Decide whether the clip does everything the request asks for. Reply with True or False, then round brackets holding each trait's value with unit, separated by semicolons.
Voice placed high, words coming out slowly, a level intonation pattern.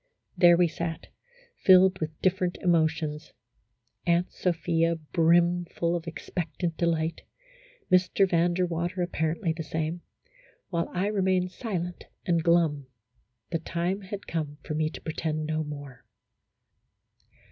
False (170 Hz; 125 wpm; 2.0 semitones)